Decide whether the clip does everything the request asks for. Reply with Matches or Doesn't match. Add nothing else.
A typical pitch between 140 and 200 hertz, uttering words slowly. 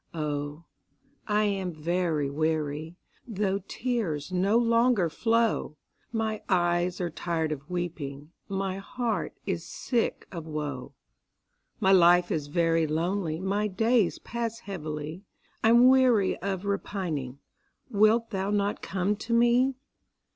Matches